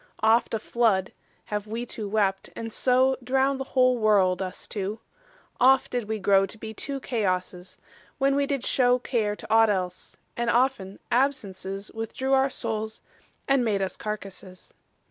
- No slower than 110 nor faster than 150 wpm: No, average, 165 wpm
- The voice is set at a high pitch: Yes, high, 220 Hz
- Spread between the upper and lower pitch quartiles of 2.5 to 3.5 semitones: No, average, 4.3 semitones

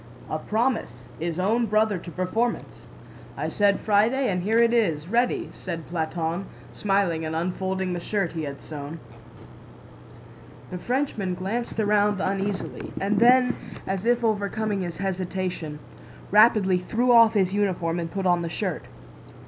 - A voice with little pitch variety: No, average, 3.8 semitones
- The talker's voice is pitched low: No, high, 195 Hz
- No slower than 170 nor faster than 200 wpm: No, average, 145 wpm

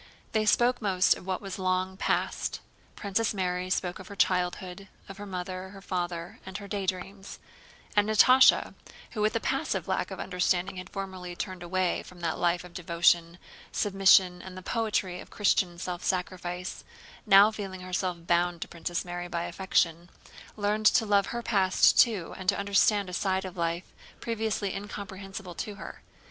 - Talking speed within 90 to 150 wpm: No, average, 170 wpm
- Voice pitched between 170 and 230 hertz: Yes, medium, 185 Hz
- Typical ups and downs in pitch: No, narrow, 2.1 semitones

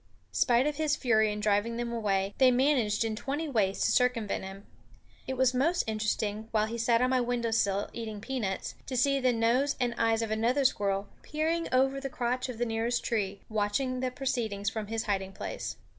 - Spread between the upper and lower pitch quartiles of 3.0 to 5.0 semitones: Yes, average, 3.3 semitones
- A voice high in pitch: Yes, high, 230 Hz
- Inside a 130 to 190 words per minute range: No, average, 200 wpm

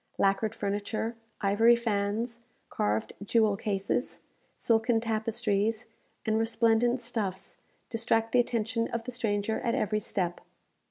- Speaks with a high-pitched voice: Yes, high, 225 Hz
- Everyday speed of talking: No, slow, 115 wpm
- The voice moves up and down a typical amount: No, narrow, 2.3 semitones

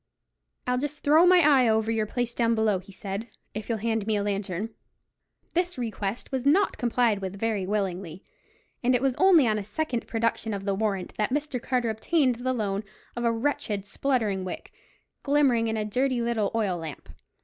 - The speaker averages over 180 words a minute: Yes, average, 190 wpm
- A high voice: Yes, high, 225 Hz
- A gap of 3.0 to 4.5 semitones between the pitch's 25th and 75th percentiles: Yes, average, 3.8 semitones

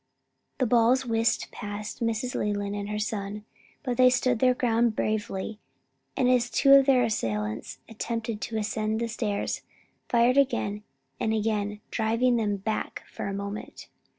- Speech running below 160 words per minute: Yes, average, 150 wpm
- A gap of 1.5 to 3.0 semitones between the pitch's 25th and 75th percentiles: Yes, average, 2.7 semitones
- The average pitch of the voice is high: Yes, high, 220 Hz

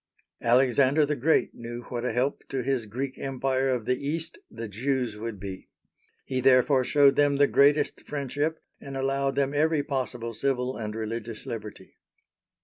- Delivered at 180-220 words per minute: No, average, 160 wpm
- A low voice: Yes, low, 130 Hz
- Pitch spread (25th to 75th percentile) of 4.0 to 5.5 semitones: No, average, 3.1 semitones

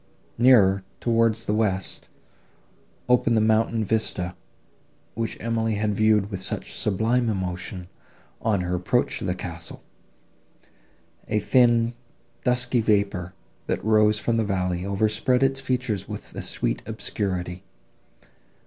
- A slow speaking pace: Yes, slow, 120 wpm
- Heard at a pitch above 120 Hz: No, low, 110 Hz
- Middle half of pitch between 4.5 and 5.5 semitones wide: No, average, 3.3 semitones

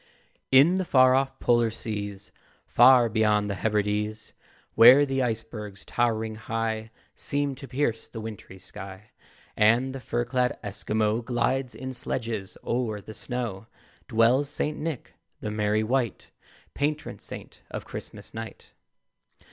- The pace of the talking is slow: Yes, slow, 130 wpm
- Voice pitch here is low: Yes, low, 115 Hz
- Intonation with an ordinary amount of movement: Yes, average, 3.3 semitones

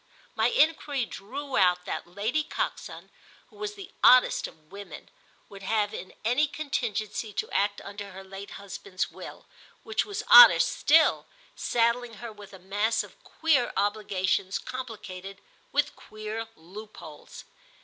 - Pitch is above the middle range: Yes, high, 215 Hz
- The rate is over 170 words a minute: No, average, 140 wpm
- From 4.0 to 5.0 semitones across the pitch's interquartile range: Yes, average, 4.6 semitones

